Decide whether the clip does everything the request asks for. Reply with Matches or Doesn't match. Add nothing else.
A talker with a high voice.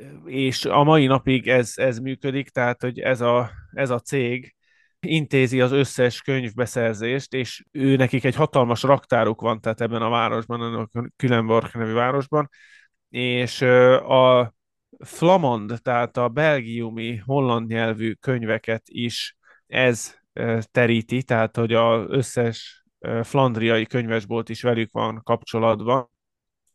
Doesn't match